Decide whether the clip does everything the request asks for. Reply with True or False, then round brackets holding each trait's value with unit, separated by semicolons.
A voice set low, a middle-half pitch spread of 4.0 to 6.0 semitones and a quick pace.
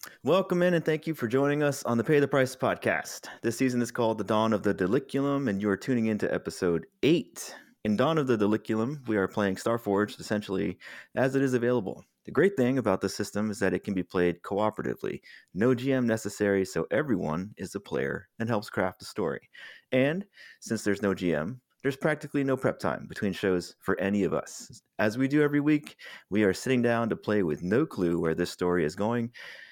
True (115 Hz; 5.0 semitones; 215 wpm)